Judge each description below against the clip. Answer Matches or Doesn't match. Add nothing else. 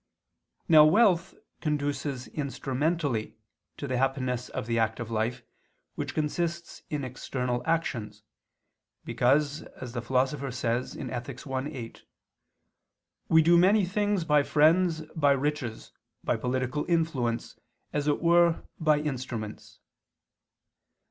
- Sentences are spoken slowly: Matches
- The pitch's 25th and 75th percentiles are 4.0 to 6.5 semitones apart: Matches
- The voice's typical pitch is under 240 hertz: Matches